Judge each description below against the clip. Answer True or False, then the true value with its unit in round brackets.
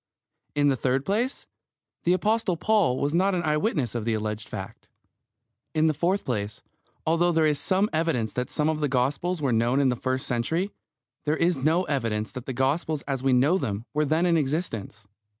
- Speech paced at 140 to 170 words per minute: False (190 wpm)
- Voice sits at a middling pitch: True (145 Hz)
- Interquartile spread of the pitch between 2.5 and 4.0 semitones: False (5.2 semitones)